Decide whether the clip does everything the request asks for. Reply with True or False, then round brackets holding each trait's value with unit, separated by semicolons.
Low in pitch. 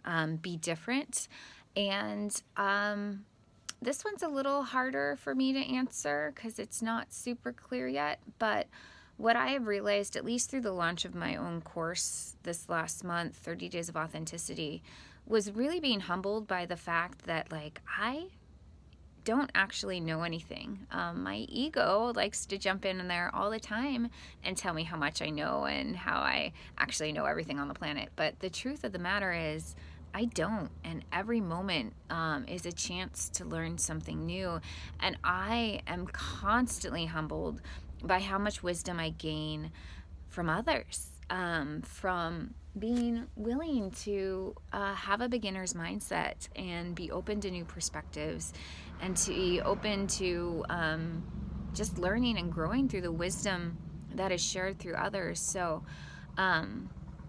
False (180 Hz)